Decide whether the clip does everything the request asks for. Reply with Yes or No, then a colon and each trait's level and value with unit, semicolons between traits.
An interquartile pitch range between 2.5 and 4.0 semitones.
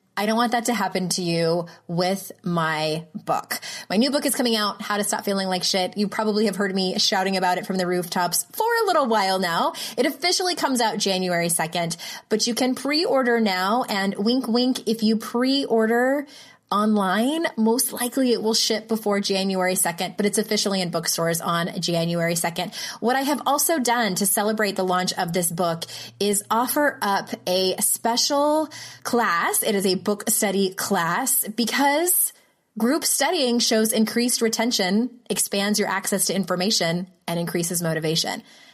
No: average, 4.6 semitones